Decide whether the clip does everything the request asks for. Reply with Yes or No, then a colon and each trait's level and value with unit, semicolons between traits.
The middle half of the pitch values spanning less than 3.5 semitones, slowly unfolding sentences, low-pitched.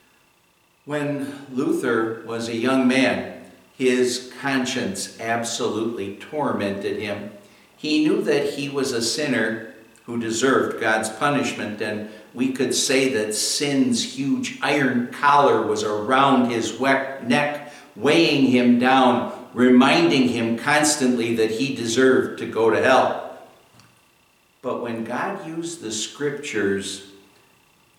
No: average, 3.8 semitones; slow, 115 wpm; low, 125 Hz